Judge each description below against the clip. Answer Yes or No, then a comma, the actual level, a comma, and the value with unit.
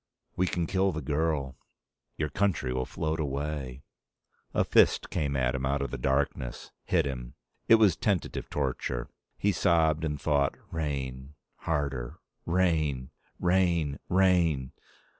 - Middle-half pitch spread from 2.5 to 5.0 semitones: Yes, average, 3.8 semitones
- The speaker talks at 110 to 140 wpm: Yes, slow, 135 wpm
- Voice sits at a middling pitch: No, very low, 75 Hz